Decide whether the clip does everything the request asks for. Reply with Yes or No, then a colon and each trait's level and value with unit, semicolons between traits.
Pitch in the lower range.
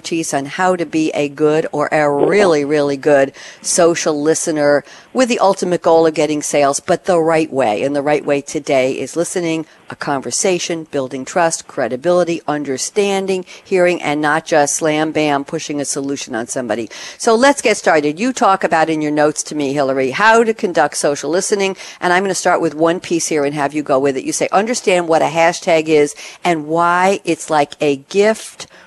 No: medium, 160 Hz